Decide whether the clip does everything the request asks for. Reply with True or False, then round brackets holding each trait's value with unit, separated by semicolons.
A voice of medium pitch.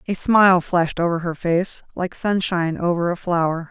True (175 Hz)